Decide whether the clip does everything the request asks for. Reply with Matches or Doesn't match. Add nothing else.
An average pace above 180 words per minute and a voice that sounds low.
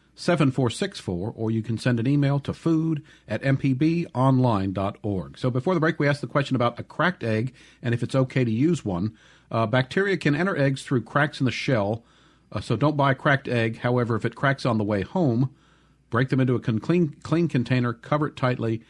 Matches